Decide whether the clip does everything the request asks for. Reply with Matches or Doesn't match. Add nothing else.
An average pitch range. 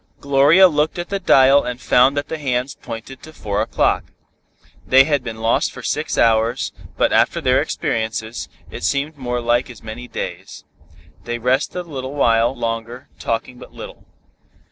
Matches